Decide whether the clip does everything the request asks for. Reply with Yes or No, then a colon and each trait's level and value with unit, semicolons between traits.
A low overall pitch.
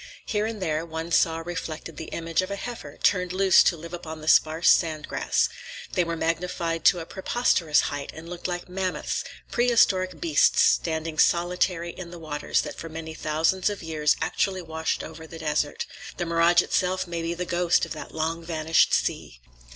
No: medium, 170 Hz